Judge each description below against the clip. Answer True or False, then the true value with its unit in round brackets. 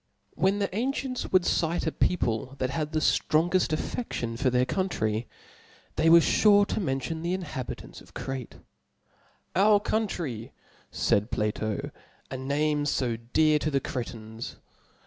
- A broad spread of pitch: True (6.7 semitones)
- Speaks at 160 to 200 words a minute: False (145 wpm)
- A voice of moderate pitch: True (150 Hz)